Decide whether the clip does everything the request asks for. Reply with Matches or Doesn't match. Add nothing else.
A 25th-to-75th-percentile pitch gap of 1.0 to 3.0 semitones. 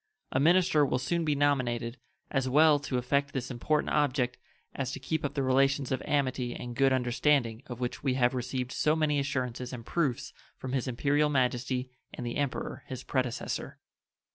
Matches